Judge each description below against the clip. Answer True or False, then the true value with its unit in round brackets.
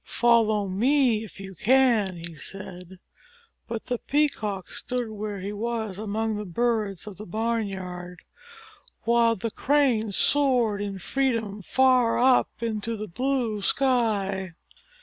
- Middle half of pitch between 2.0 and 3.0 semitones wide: False (3.4 semitones)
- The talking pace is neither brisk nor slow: False (130 wpm)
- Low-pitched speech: False (220 Hz)